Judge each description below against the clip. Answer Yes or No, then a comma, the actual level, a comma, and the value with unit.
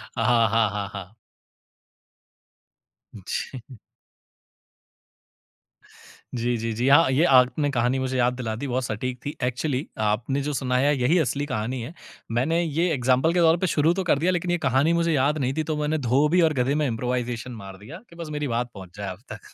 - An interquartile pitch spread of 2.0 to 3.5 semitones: No, average, 4.3 semitones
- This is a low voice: Yes, low, 130 Hz